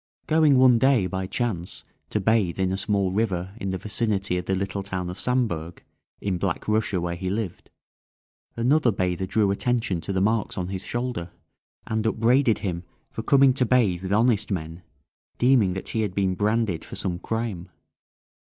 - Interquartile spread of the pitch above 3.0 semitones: Yes, average, 3.8 semitones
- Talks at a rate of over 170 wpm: Yes, average, 180 wpm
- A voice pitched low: Yes, low, 100 Hz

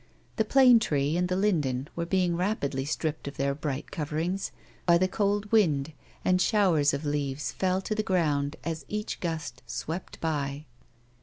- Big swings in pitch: No, average, 4.7 semitones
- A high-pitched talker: No, medium, 165 Hz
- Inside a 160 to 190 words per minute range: Yes, average, 165 wpm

